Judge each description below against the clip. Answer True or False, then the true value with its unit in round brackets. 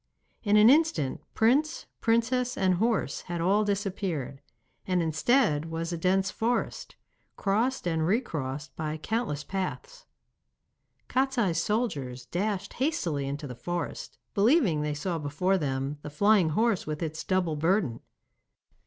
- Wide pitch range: True (6.6 semitones)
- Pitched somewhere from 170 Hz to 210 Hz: True (185 Hz)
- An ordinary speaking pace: False (130 wpm)